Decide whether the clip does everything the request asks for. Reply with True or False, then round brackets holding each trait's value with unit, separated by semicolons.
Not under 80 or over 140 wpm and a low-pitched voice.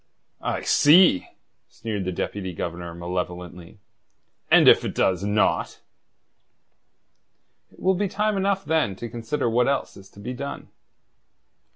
True (135 wpm; 110 Hz)